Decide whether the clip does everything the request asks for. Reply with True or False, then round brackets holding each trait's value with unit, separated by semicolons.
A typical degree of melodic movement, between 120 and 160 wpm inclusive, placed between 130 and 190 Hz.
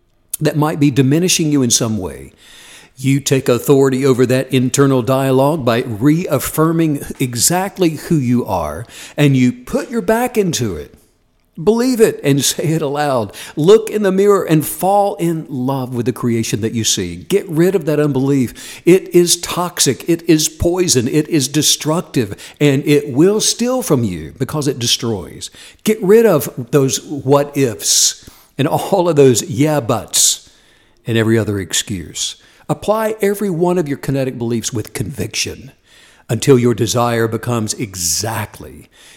False (5.8 semitones; 155 wpm; 140 Hz)